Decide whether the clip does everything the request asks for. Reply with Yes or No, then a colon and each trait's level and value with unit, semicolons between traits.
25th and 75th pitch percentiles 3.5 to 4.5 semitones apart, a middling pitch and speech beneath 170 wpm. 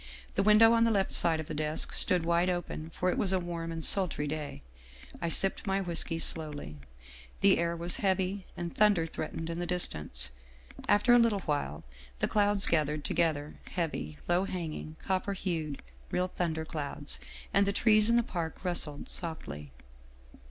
No: average, 3.8 semitones; medium, 170 Hz; average, 175 wpm